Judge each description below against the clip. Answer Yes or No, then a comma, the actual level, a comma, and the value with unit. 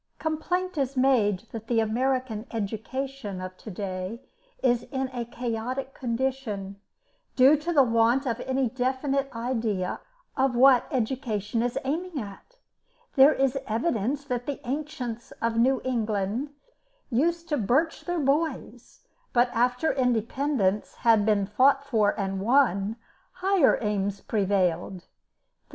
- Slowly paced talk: Yes, slow, 130 wpm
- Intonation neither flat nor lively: Yes, average, 4.0 semitones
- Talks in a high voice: Yes, high, 245 Hz